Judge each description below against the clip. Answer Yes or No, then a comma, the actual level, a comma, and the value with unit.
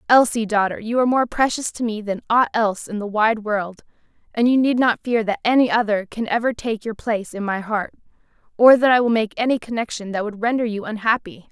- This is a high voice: Yes, high, 225 Hz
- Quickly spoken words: Yes, fast, 225 wpm